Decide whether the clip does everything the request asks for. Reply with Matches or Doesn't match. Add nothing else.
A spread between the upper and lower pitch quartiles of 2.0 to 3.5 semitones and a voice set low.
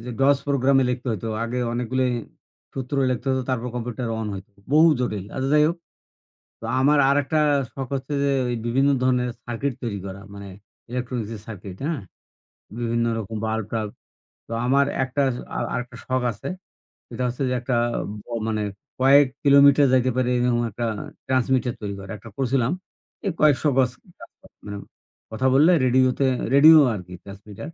Matches